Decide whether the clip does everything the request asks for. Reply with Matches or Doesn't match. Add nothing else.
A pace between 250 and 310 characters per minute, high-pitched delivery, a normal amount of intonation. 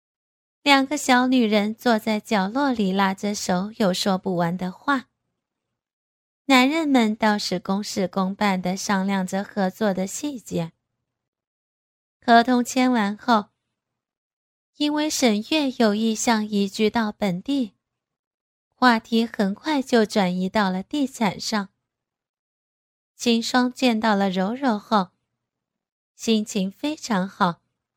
Doesn't match